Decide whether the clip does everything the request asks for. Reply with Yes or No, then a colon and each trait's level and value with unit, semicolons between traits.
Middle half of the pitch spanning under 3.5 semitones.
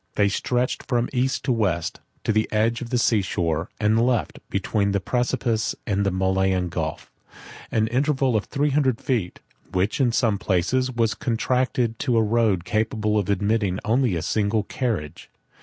No: average, 3.9 semitones